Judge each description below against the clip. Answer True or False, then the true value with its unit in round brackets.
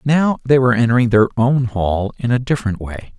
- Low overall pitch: True (120 Hz)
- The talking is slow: False (205 wpm)